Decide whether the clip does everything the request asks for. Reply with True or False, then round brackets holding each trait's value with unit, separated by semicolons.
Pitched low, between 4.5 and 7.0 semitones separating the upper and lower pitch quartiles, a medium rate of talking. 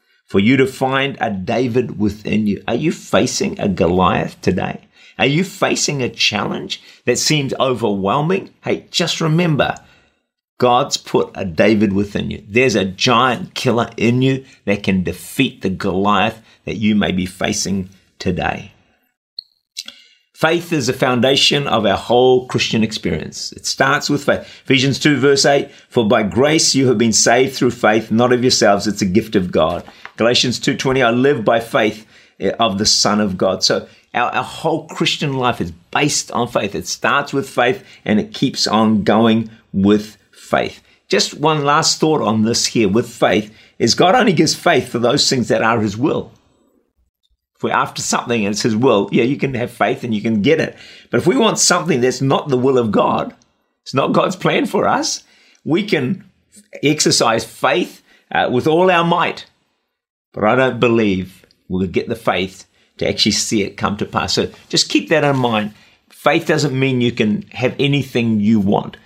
True (125 Hz; 4.8 semitones; 180 wpm)